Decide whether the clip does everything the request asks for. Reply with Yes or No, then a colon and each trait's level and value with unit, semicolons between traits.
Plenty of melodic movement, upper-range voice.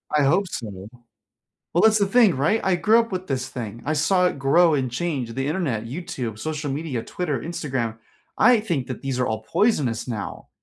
No: wide, 6.4 semitones; medium, 145 Hz